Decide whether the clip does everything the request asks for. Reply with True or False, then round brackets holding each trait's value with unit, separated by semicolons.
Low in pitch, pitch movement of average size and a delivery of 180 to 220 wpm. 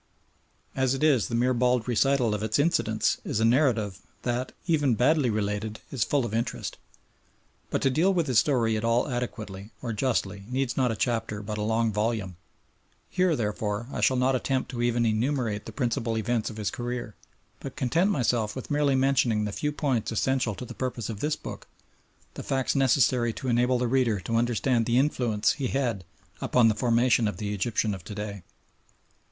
True (120 Hz; 3.3 semitones; 190 wpm)